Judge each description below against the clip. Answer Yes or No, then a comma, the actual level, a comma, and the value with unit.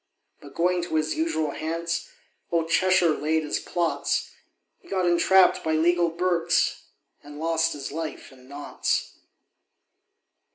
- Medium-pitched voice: Yes, medium, 165 Hz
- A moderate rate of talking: No, slow, 130 wpm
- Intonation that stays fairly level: Yes, narrow, 1.9 semitones